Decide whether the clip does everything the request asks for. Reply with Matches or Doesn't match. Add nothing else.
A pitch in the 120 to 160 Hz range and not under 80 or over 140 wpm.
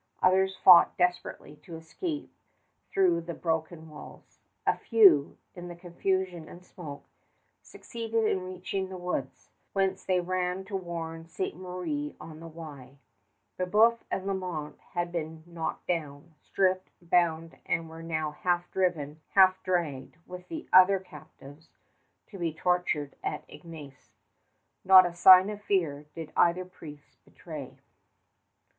Doesn't match